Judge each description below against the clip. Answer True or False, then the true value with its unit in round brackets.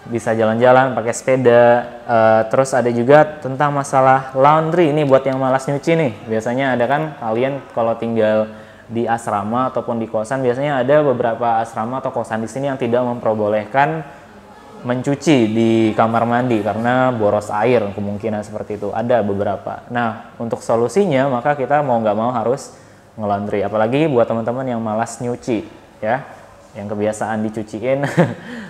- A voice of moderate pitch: False (120 Hz)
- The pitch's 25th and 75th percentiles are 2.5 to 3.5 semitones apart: True (3.2 semitones)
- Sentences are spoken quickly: True (150 wpm)